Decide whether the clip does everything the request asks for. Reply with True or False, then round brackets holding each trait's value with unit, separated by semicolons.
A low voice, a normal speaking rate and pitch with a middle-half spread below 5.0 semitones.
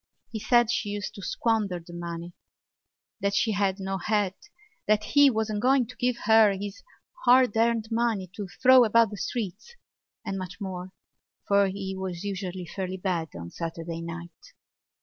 False (200 Hz; 170 wpm; 3.4 semitones)